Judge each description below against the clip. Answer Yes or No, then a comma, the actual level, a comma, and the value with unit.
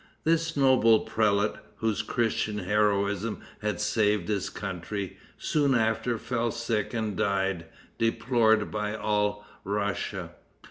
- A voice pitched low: Yes, low, 105 Hz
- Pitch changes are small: Yes, narrow, 2.0 semitones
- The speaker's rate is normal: No, slow, 110 wpm